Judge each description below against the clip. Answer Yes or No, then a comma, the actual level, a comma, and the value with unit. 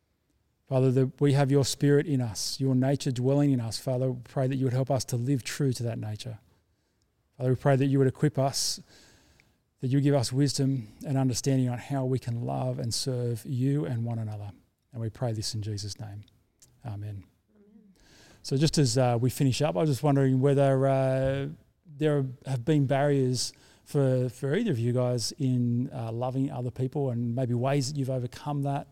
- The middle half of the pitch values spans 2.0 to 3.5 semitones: Yes, narrow, 2.5 semitones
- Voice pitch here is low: Yes, low, 130 Hz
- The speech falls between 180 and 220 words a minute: Yes, average, 200 wpm